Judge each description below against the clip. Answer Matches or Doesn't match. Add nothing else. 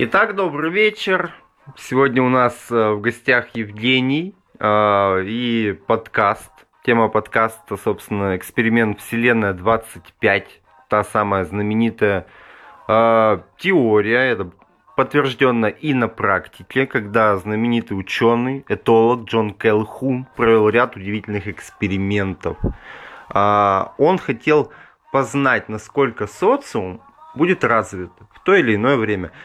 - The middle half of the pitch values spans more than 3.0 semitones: Matches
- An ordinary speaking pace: Doesn't match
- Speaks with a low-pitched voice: Matches